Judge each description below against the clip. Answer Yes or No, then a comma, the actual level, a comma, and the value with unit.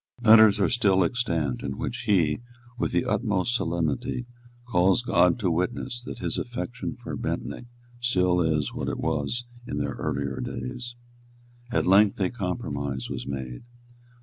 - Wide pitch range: Yes, wide, 7.8 semitones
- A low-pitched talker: Yes, very low, 95 Hz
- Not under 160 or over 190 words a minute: No, average, 150 wpm